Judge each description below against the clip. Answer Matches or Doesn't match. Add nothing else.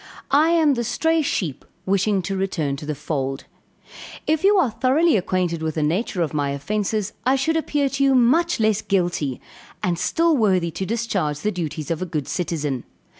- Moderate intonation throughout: Doesn't match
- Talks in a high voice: Matches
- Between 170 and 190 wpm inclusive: Matches